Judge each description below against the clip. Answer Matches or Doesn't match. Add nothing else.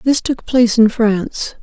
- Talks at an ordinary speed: Matches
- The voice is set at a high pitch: Matches